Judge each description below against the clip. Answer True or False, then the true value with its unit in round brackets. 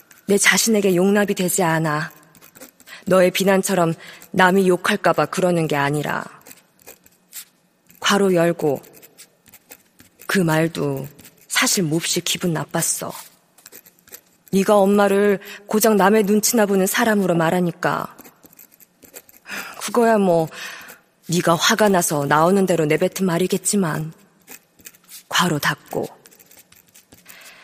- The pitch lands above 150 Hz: True (185 Hz)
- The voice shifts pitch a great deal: False (3.3 semitones)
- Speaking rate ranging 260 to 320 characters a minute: False (210 characters per minute)